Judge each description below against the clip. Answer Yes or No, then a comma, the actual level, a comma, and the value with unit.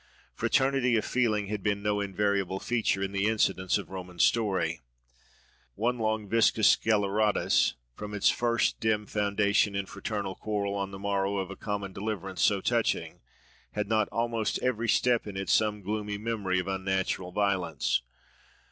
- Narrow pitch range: Yes, narrow, 2.0 semitones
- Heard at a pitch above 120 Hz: No, low, 105 Hz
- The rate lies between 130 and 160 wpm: Yes, average, 150 wpm